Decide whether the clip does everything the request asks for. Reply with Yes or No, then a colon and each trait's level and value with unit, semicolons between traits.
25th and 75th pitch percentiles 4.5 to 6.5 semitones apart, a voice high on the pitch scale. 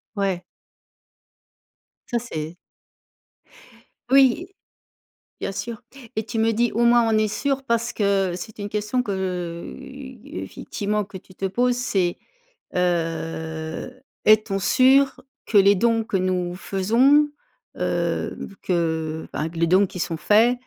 Yes: average, 4.8 semitones; high, 205 Hz